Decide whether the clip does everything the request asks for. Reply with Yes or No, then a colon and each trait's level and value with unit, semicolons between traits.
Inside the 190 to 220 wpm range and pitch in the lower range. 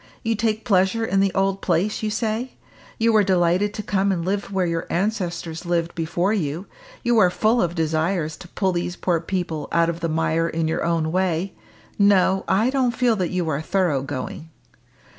No: average, 195 wpm; medium, 185 Hz